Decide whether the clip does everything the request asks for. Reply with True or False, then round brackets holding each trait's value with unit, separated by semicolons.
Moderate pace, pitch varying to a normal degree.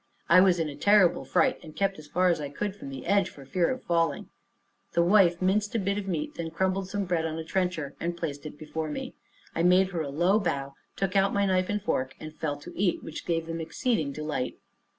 False (240 wpm; 3.7 semitones)